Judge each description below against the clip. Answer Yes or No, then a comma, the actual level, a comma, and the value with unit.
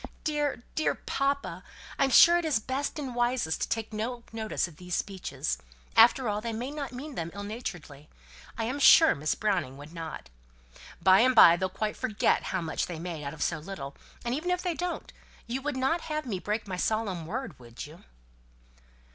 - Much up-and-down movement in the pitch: Yes, wide, 7.4 semitones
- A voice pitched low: No, high, 220 Hz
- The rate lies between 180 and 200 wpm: Yes, average, 195 wpm